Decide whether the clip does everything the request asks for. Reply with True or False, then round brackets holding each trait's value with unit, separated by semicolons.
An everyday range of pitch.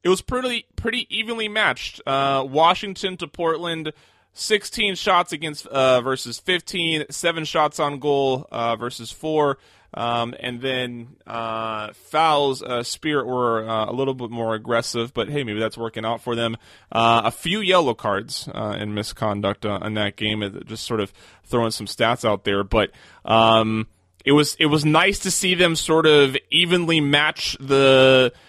False (6.1 semitones)